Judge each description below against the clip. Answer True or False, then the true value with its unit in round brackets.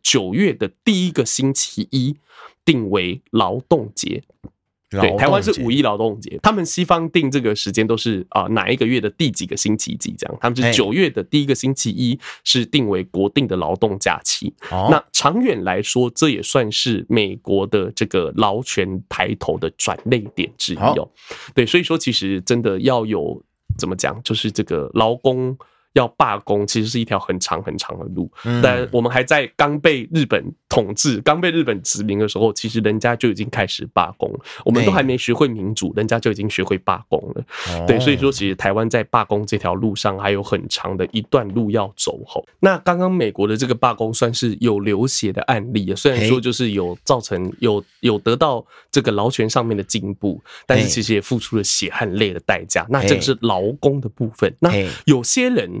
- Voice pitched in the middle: False (115 Hz)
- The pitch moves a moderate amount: True (4.2 semitones)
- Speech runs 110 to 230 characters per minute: False (290 characters per minute)